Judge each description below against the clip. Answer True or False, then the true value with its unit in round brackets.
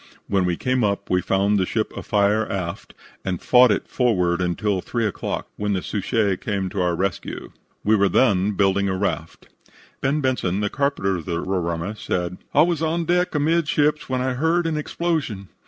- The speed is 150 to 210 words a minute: True (185 wpm)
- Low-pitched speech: True (105 Hz)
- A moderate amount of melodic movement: False (5.8 semitones)